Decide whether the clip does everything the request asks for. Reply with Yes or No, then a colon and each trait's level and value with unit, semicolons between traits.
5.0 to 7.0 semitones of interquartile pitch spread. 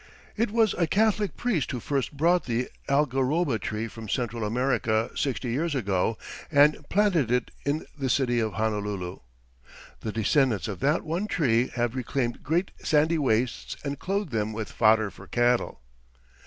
Yes: wide, 5.6 semitones